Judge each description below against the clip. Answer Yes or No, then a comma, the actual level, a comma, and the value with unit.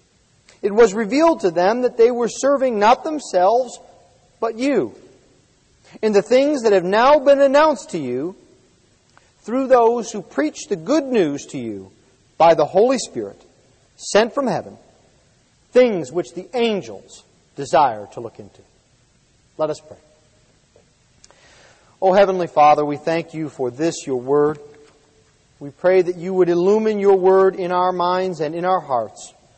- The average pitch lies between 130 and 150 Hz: No, medium, 185 Hz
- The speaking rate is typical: Yes, average, 155 wpm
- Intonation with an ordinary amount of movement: No, wide, 7.5 semitones